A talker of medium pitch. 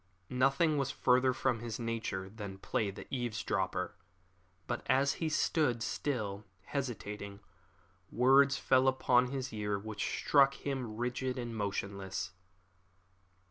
No: low, 120 Hz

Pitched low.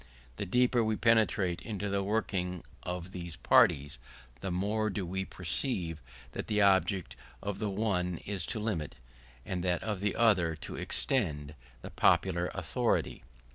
Yes: very low, 95 Hz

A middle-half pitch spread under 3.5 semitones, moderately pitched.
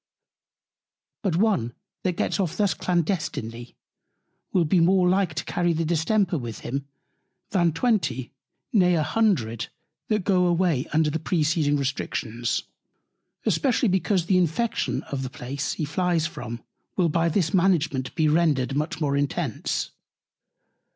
No: average, 4.4 semitones; medium, 165 Hz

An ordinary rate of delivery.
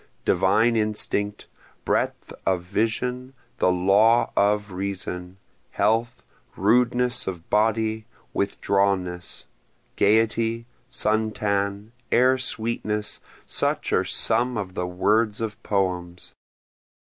No: slow, 95 wpm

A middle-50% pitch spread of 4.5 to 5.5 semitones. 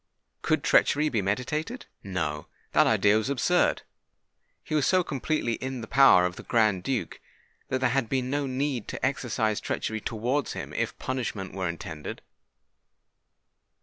Yes: average, 4.9 semitones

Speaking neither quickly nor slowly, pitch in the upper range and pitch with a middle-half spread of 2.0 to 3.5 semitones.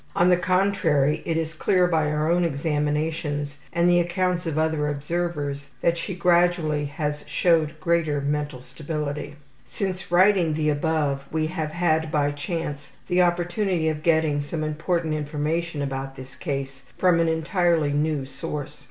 No: average, 150 wpm; medium, 155 Hz; average, 2.7 semitones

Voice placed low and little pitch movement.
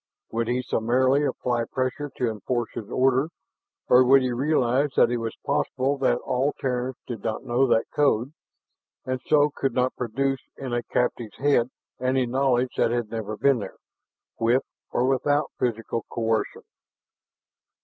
Yes: low, 125 Hz; narrow, 2.3 semitones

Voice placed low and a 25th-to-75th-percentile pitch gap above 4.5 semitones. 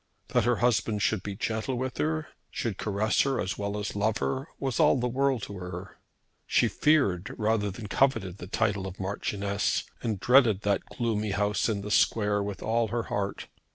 No: low, 105 Hz; average, 3.1 semitones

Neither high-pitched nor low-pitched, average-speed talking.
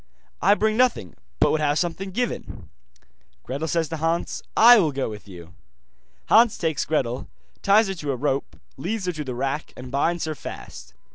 Yes: medium, 160 Hz; average, 185 wpm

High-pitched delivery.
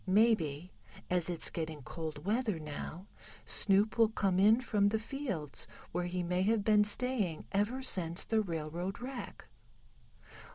Yes: high, 195 Hz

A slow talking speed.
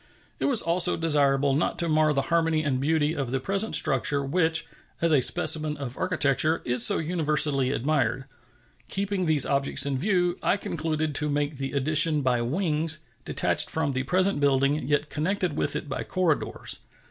No: average, 170 wpm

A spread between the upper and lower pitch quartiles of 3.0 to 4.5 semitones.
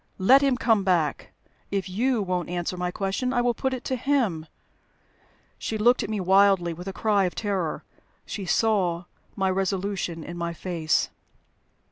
Yes: average, 3.9 semitones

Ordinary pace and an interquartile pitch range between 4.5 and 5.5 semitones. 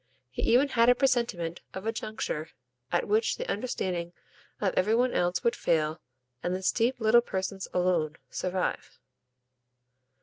Yes: average, 145 wpm; average, 4.9 semitones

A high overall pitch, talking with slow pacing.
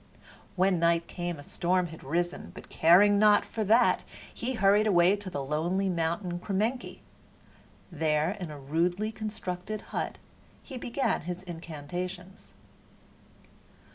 No: medium, 180 Hz; slow, 130 wpm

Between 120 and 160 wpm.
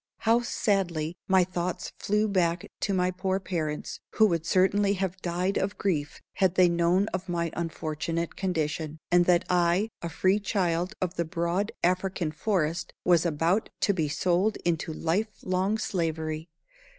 Yes: average, 155 wpm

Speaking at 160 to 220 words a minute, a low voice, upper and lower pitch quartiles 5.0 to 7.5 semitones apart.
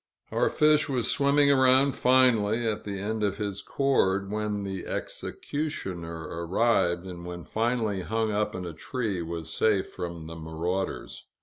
No: average, 150 wpm; low, 105 Hz; wide, 5.4 semitones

